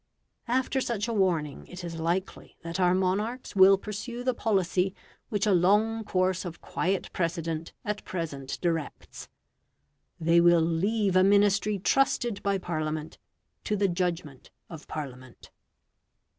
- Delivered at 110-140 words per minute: Yes, slow, 135 wpm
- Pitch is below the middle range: No, medium, 185 Hz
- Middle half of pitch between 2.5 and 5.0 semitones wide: Yes, average, 3.7 semitones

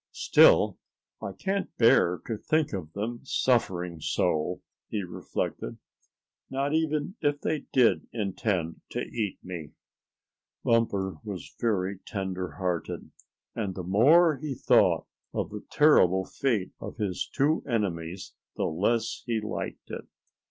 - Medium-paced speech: No, slow, 130 wpm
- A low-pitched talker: Yes, low, 105 Hz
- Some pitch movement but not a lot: No, wide, 6.4 semitones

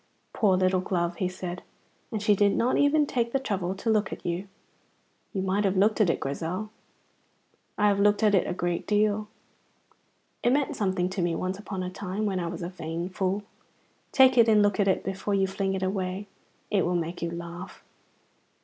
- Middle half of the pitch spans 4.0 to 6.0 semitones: No, narrow, 2.5 semitones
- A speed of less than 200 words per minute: No, fast, 205 wpm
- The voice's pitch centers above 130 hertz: Yes, high, 190 Hz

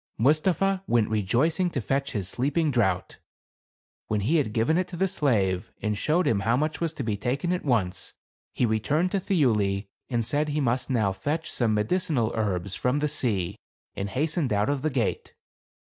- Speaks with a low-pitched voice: Yes, low, 125 Hz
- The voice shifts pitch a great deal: Yes, wide, 6.5 semitones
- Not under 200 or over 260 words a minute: No, average, 185 wpm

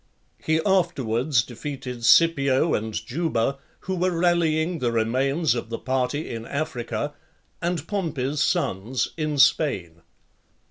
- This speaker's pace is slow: Yes, slow, 120 wpm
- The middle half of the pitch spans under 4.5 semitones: No, wide, 5.6 semitones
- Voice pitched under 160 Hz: Yes, medium, 140 Hz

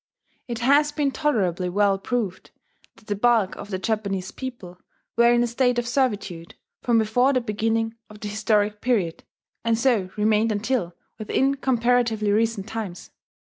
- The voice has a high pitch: Yes, high, 225 Hz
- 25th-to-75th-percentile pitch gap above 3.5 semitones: No, average, 3.0 semitones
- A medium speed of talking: Yes, average, 155 wpm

